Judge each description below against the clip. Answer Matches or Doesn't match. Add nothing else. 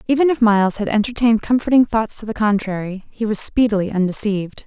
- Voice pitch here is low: Doesn't match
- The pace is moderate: Matches